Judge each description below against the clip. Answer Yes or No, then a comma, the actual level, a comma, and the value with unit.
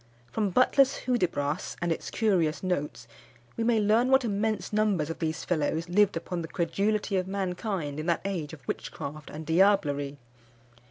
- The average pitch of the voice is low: No, medium, 180 Hz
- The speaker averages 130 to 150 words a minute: No, average, 160 wpm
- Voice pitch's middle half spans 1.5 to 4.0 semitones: No, average, 4.9 semitones